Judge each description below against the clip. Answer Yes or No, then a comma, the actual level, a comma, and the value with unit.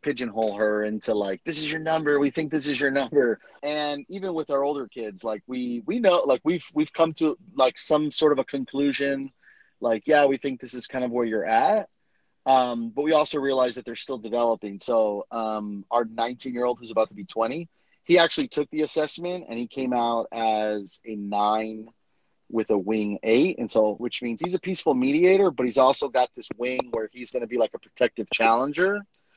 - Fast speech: Yes, fast, 215 wpm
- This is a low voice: Yes, low, 130 Hz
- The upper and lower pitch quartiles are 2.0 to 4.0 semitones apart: No, average, 4.9 semitones